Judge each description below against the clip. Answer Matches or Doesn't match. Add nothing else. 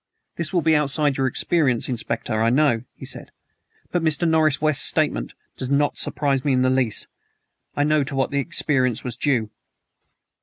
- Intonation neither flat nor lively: Matches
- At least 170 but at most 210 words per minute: Matches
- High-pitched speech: Doesn't match